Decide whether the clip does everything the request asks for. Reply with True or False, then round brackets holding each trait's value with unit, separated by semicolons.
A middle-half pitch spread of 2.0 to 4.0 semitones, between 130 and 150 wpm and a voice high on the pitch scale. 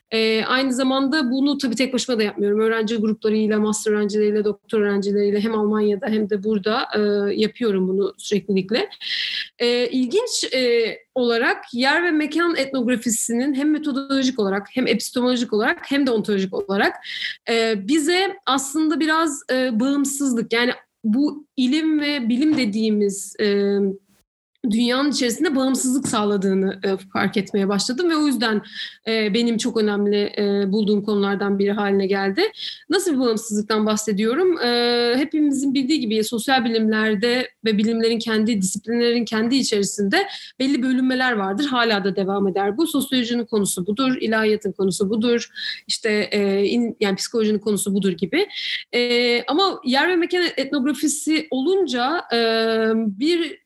False (4.4 semitones; 140 wpm; 230 Hz)